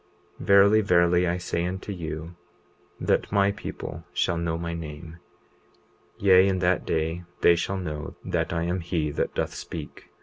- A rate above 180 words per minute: No, average, 165 wpm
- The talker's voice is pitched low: Yes, very low, 85 Hz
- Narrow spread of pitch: Yes, narrow, 2.2 semitones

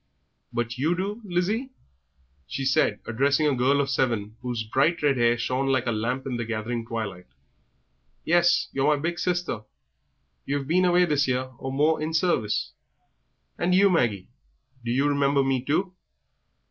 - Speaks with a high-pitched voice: No, low, 135 Hz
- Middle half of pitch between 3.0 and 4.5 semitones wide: No, wide, 5.6 semitones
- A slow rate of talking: No, average, 160 wpm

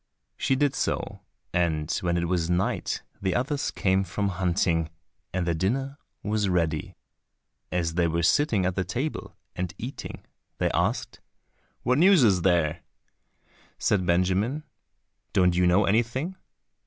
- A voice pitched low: Yes, very low, 95 Hz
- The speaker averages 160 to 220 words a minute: No, average, 140 wpm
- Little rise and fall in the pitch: No, wide, 5.4 semitones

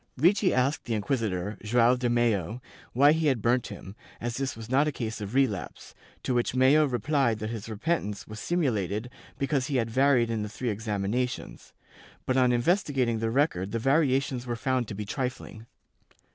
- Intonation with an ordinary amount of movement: Yes, average, 3.6 semitones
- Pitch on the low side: Yes, low, 120 Hz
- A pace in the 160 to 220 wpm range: Yes, average, 180 wpm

